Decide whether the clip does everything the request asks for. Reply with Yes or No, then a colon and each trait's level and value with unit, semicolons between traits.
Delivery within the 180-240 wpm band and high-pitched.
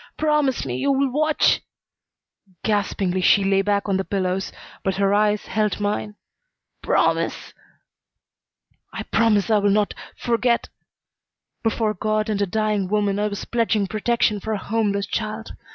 No: average, 150 wpm; high, 210 Hz